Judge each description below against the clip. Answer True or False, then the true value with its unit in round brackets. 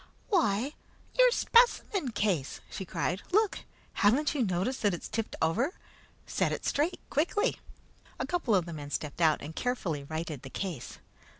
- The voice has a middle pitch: False (210 Hz)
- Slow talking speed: False (160 wpm)